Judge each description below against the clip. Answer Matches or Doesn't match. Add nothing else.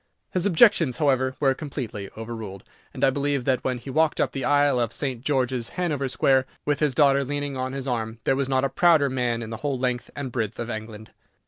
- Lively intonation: Doesn't match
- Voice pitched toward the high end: Doesn't match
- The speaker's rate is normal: Doesn't match